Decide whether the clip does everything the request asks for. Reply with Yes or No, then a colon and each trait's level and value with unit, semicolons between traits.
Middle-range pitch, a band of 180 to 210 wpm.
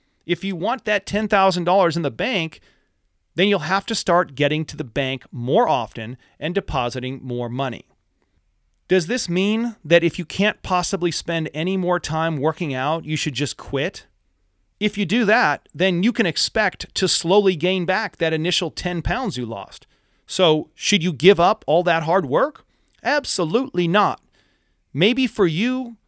No: medium, 175 Hz; average, 170 wpm